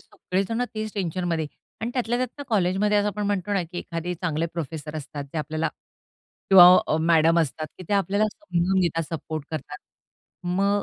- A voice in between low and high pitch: Yes, medium, 180 Hz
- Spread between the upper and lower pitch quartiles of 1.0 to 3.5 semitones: No, average, 4.1 semitones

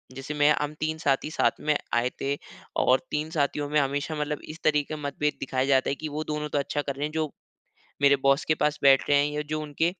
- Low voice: No, medium, 145 Hz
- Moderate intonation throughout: No, narrow, 1.4 semitones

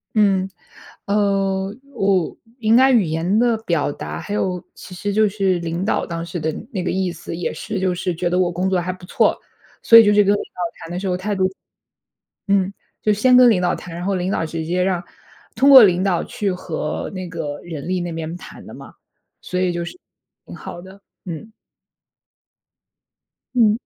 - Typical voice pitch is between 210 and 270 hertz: No, medium, 185 Hz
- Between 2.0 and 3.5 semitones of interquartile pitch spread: Yes, average, 2.8 semitones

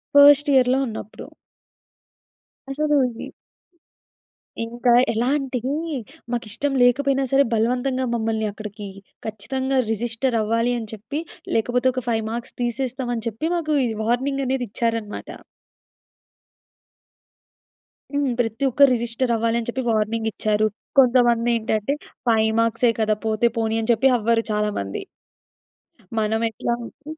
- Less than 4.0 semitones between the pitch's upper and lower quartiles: Yes, average, 2.9 semitones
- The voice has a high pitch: Yes, high, 235 Hz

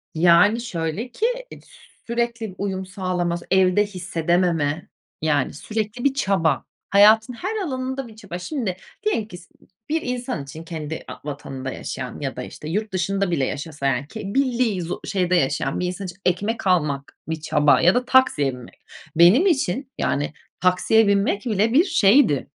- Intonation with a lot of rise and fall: Yes, wide, 5.8 semitones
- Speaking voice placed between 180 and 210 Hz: Yes, high, 190 Hz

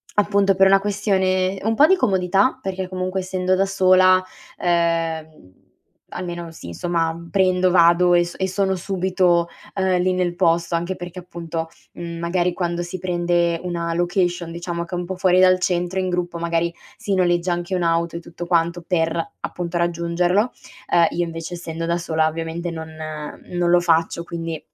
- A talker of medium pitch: Yes, medium, 175 Hz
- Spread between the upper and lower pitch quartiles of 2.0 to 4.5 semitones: No, narrow, 1.6 semitones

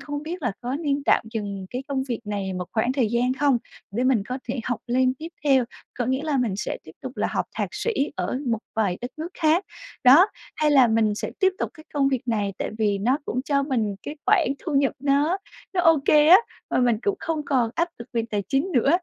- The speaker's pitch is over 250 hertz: Yes, very high, 260 Hz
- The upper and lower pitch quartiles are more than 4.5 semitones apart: No, average, 4.2 semitones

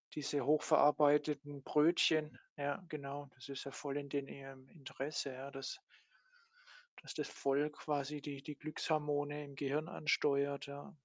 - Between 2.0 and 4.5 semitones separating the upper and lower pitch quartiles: No, narrow, 1.3 semitones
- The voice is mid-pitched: Yes, medium, 145 Hz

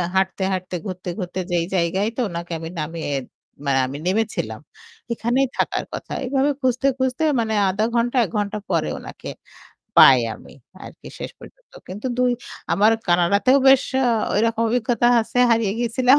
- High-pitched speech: Yes, high, 215 Hz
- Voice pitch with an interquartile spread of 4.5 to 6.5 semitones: Yes, wide, 5.4 semitones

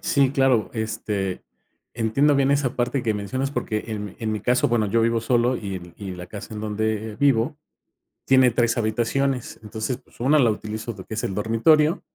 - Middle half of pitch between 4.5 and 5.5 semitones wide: No, average, 3.5 semitones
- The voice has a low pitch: Yes, low, 115 Hz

